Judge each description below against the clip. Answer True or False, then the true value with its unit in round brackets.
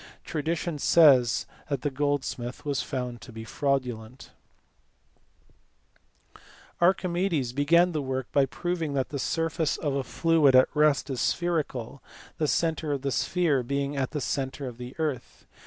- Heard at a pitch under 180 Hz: True (140 Hz)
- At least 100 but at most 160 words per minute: True (155 wpm)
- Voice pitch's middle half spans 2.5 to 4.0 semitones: True (3.6 semitones)